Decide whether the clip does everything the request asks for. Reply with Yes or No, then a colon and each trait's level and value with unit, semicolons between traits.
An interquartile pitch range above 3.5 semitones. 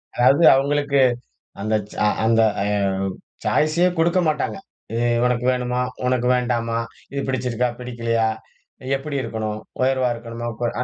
No: average, 3.1 semitones